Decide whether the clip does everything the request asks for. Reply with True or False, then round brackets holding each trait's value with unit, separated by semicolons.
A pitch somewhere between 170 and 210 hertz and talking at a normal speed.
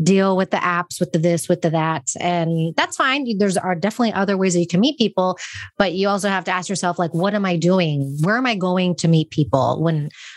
False (185 Hz; 250 wpm)